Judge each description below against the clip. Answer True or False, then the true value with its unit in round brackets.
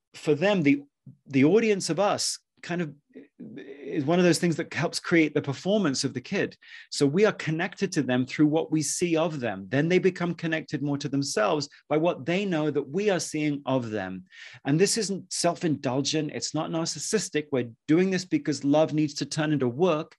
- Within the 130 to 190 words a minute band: False (200 wpm)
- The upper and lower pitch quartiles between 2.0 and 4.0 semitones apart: True (3.6 semitones)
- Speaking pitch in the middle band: True (155 Hz)